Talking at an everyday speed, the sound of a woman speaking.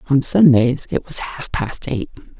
Yes: average, 175 wpm; female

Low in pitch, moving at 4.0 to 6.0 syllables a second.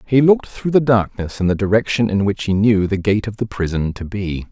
Yes: low, 105 Hz; 5.5 syllables/s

